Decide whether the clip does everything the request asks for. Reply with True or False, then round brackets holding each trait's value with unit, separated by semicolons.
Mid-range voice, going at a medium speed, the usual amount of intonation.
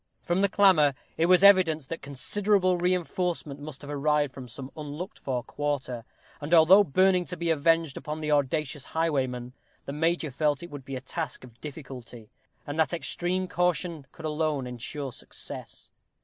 True (150 Hz; 165 wpm; 3.9 semitones)